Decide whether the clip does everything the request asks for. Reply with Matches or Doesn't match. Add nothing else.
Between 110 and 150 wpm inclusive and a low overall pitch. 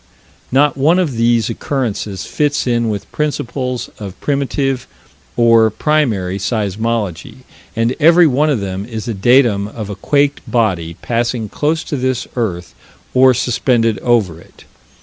Matches